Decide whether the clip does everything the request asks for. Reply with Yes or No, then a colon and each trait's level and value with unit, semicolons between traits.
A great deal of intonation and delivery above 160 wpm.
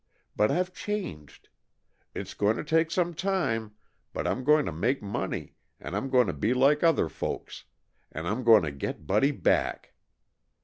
Yes: wide, 7.5 semitones; average, 170 wpm